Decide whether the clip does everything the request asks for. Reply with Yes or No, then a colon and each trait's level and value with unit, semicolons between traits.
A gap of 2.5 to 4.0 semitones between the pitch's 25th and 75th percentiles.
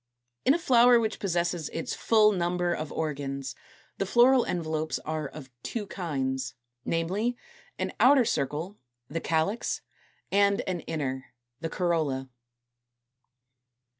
No: wide, 5.4 semitones